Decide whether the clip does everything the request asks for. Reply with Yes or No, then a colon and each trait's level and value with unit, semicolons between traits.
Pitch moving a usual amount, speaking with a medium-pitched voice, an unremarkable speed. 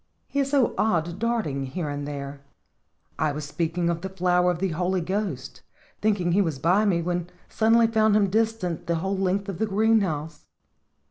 Yes: average, 4.4 semitones; medium, 180 Hz; average, 190 wpm